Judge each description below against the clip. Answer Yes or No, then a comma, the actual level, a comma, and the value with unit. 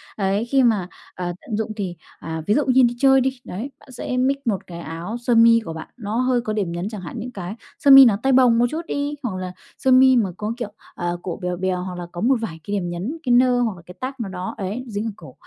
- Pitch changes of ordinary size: No, wide, 5.7 semitones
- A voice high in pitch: Yes, high, 220 Hz